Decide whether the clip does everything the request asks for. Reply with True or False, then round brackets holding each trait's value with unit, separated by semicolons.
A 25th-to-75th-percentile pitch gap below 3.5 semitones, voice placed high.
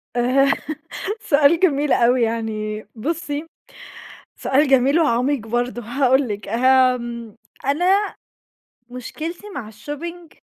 False (4.0 semitones; 260 Hz)